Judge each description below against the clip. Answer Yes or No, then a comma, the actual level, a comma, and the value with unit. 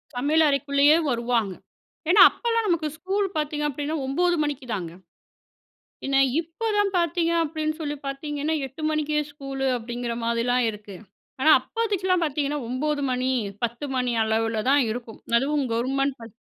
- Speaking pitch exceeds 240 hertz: Yes, very high, 285 Hz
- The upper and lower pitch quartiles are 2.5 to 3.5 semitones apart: No, average, 4.2 semitones